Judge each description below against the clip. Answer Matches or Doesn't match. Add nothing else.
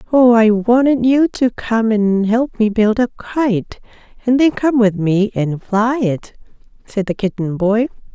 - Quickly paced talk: Doesn't match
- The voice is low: Doesn't match